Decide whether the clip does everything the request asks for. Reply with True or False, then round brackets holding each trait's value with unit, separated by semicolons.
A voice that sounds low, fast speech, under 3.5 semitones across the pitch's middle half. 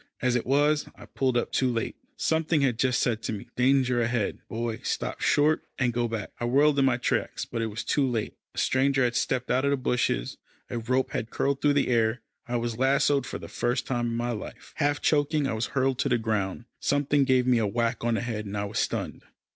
True (125 Hz; 235 wpm; 2.8 semitones)